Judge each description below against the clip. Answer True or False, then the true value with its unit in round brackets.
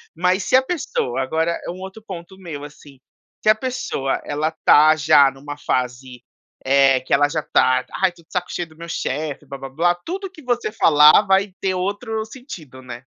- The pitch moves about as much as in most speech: False (6.0 semitones)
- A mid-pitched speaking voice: True (160 Hz)